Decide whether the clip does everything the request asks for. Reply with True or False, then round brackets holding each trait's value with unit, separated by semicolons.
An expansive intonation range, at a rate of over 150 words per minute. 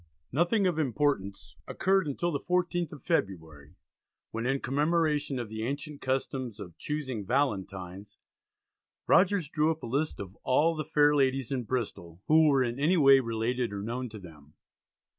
True (5.7 semitones; 160 wpm)